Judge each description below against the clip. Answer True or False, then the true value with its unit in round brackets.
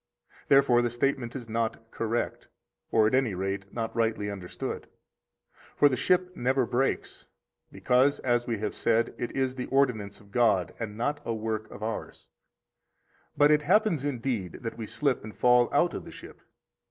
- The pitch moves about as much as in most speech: True (3.4 semitones)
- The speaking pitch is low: True (120 Hz)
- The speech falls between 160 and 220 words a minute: True (170 wpm)